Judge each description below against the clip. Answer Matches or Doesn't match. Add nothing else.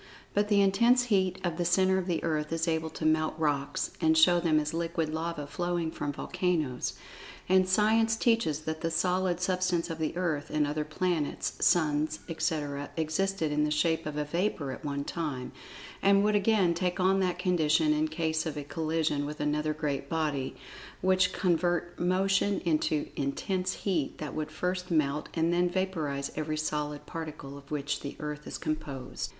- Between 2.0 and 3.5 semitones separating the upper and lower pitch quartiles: Matches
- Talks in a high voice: Doesn't match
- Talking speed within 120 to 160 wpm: Doesn't match